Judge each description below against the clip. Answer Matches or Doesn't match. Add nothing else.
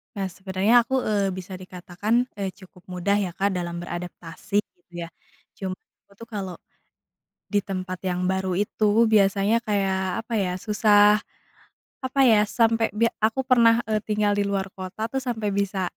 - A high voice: Matches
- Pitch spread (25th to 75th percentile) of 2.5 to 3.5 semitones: Matches